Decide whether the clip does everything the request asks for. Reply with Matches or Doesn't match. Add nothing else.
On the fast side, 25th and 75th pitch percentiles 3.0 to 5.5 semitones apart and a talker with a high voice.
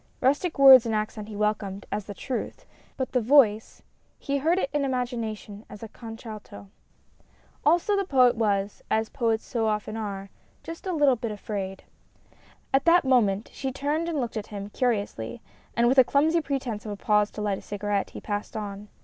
Doesn't match